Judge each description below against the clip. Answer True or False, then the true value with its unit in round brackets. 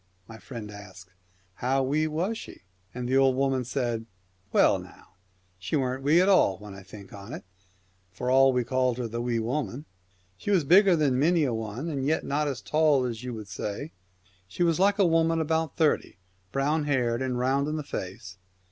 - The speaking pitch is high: False (130 Hz)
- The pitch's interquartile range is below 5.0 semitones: False (5.5 semitones)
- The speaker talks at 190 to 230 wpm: True (200 wpm)